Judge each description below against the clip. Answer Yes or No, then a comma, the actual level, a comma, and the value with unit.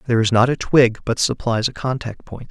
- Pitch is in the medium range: No, low, 120 Hz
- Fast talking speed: Yes, fast, 240 wpm